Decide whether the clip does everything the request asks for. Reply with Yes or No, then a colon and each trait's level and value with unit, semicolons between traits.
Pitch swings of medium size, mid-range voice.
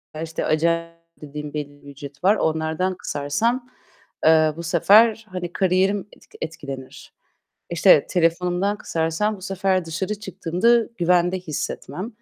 Yes: average, 3.3 semitones; medium, 170 Hz